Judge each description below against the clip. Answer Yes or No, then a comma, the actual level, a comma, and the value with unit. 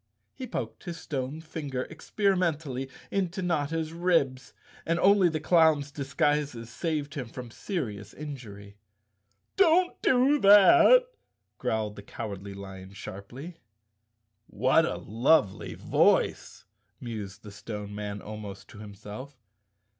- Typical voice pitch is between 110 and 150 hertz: Yes, low, 135 Hz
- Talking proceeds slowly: Yes, slow, 120 wpm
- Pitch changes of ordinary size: No, wide, 7.8 semitones